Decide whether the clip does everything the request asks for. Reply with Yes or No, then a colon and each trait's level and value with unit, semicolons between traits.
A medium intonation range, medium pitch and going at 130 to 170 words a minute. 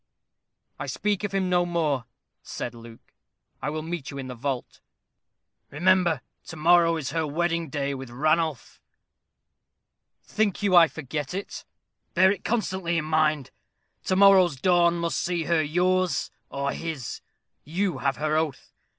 Yes: average, 3.7 semitones; medium, 165 Hz; average, 150 wpm